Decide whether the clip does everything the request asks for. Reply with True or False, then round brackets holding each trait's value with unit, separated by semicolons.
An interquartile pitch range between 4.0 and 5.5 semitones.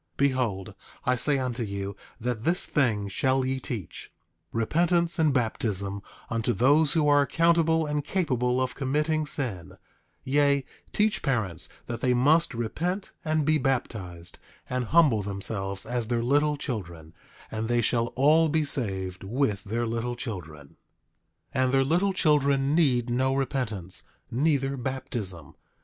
True (4.9 semitones)